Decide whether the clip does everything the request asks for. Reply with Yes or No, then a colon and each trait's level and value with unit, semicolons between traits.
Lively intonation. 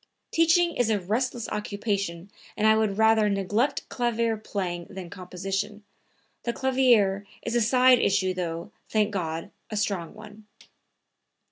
No: average, 3.3 semitones